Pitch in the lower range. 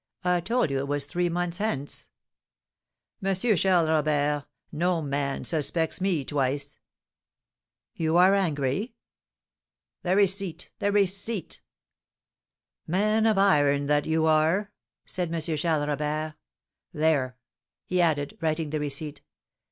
No: medium, 160 Hz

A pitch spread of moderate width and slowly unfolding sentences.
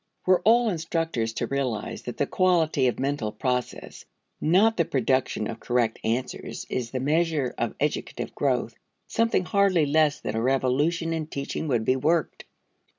No: average, 5.0 semitones; average, 155 wpm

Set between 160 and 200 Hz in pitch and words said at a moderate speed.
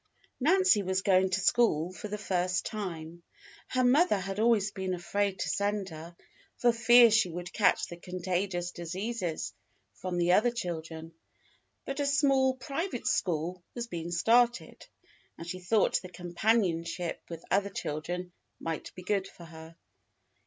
Yes: medium, 185 Hz; average, 150 wpm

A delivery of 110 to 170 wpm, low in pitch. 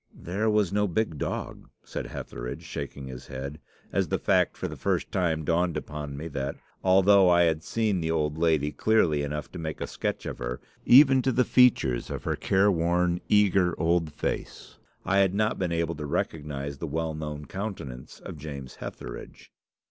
No: average, 185 wpm; very low, 80 Hz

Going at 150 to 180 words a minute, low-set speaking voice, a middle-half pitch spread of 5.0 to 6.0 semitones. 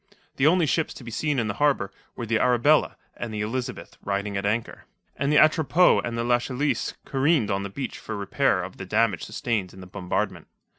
No: fast, 205 wpm; low, 115 Hz; wide, 5.6 semitones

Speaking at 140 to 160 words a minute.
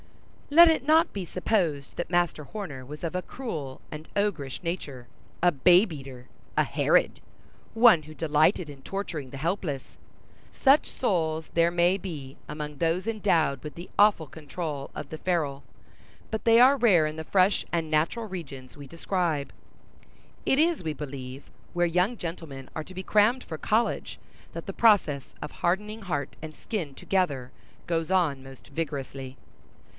Yes: average, 155 wpm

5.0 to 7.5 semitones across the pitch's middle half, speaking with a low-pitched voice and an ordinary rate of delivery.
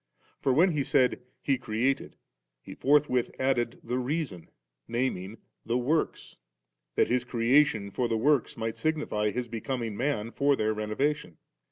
No: average, 3.8 semitones; low, 125 Hz; average, 150 wpm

